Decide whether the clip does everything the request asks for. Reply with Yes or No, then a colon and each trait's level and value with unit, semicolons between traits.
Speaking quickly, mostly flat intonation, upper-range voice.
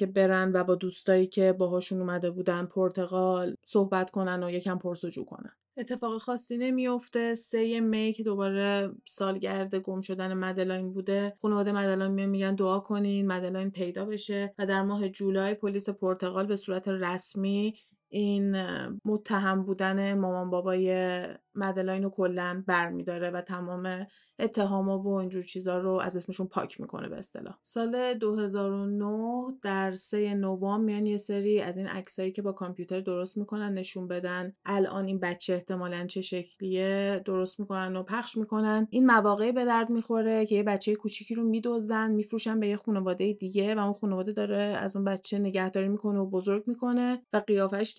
Yes: fast, 160 wpm; narrow, 2.1 semitones; high, 195 Hz